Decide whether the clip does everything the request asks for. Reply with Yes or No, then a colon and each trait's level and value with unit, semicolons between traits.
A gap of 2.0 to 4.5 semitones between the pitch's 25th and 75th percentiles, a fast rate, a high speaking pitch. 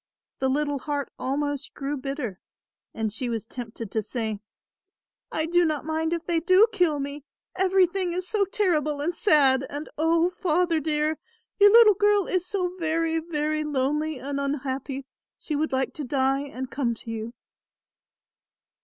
No: average, 4.1 semitones; average, 160 wpm; very high, 300 Hz